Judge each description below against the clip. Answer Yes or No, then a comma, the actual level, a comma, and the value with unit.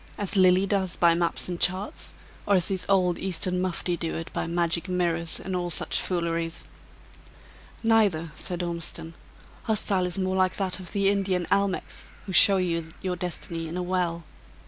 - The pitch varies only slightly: Yes, narrow, 2.1 semitones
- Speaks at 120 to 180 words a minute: Yes, average, 175 wpm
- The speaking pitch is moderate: Yes, medium, 180 Hz